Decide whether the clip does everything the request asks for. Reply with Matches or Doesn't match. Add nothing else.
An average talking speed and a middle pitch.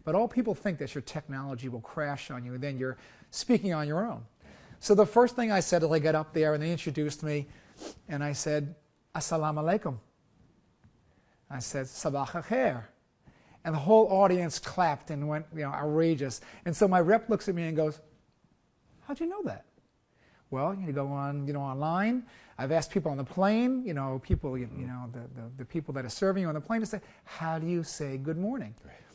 Doesn't match